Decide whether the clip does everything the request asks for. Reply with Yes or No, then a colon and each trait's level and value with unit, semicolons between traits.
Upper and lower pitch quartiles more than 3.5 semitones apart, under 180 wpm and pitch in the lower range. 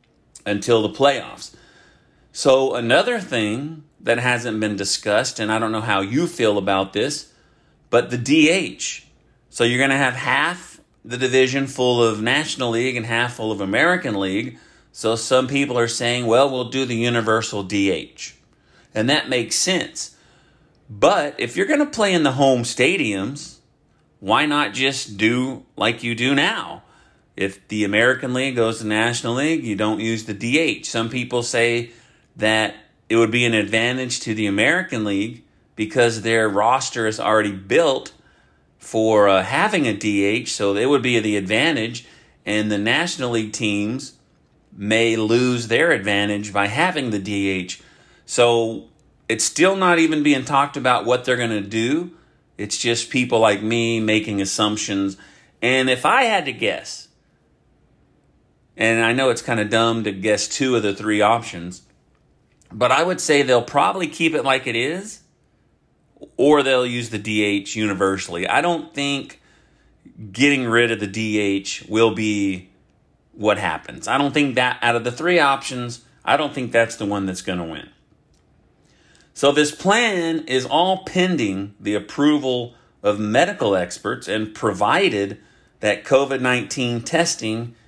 Yes: average, 3.9 semitones; average, 160 wpm; low, 115 Hz